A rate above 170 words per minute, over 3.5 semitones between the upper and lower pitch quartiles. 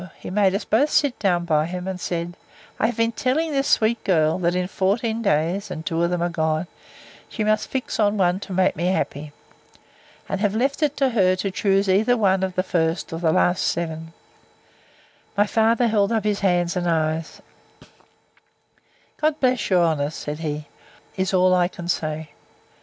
Yes: average, 185 wpm; average, 4.1 semitones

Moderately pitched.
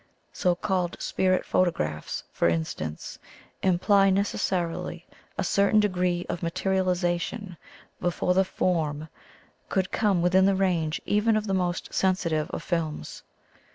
Yes: medium, 180 Hz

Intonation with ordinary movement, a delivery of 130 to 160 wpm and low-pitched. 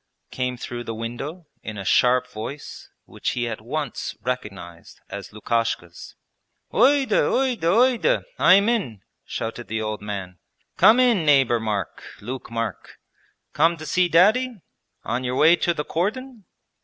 No: wide, 8.7 semitones; average, 145 wpm; low, 130 Hz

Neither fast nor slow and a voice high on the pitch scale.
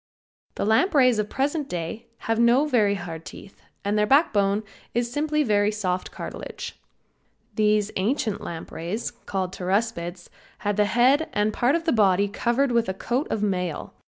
Yes: average, 160 wpm; high, 215 Hz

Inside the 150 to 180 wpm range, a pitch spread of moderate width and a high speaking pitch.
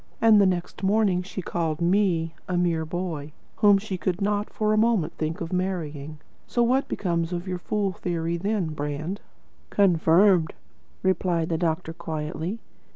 No: average, 155 wpm; average, 3.4 semitones; medium, 180 Hz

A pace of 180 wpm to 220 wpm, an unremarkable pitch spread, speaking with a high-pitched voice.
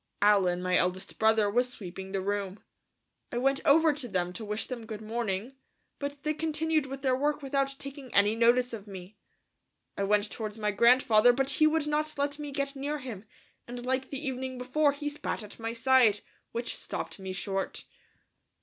Yes: average, 185 wpm; average, 5.0 semitones; high, 245 Hz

